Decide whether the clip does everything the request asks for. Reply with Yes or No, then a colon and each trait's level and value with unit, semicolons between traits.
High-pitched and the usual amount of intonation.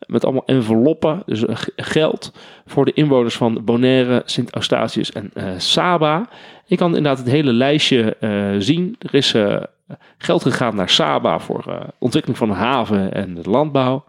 No: low, 130 Hz; average, 4.9 semitones